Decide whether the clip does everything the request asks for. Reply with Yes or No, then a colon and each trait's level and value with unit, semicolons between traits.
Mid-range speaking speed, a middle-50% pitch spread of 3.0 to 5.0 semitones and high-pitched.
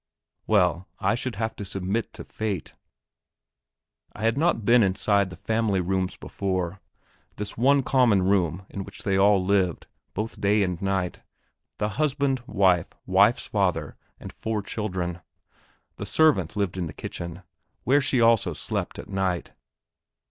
No: average, 150 wpm; average, 3.3 semitones; low, 100 Hz